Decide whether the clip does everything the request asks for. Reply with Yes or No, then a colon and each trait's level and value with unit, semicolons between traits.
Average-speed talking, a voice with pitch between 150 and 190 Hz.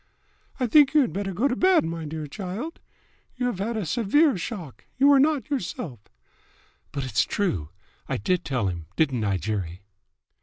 Yes: average, 180 wpm; medium, 185 Hz